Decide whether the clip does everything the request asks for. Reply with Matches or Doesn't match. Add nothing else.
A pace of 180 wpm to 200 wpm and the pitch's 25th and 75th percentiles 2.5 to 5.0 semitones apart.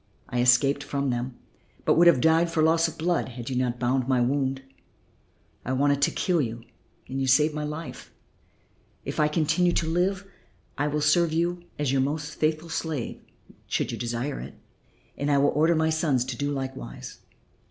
Matches